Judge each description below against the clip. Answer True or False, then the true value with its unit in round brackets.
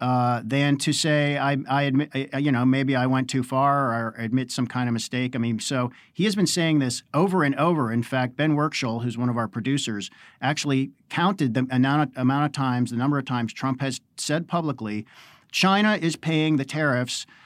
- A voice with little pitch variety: False (3.1 semitones)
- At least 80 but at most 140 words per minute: False (205 wpm)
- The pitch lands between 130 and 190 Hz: True (135 Hz)